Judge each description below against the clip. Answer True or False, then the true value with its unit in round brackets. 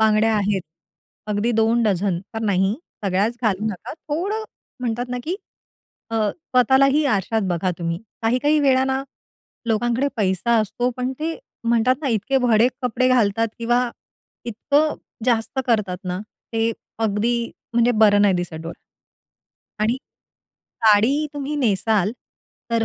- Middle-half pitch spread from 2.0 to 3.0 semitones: False (3.5 semitones)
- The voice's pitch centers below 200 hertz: False (230 Hz)